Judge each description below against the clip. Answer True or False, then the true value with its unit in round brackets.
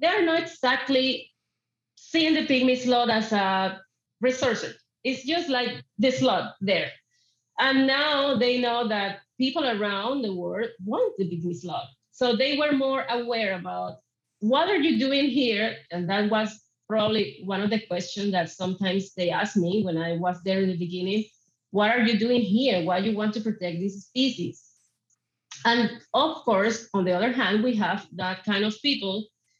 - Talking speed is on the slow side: False (175 wpm)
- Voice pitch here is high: True (220 Hz)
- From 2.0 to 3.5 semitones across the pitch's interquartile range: False (5.0 semitones)